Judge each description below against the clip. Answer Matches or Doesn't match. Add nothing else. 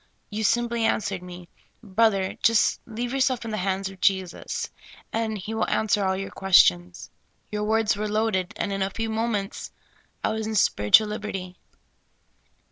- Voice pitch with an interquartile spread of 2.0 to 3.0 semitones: Matches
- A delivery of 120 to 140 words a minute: Doesn't match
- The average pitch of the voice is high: Matches